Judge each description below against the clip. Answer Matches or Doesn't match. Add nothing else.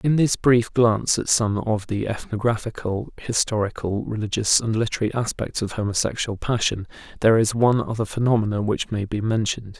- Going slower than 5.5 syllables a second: Doesn't match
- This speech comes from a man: Matches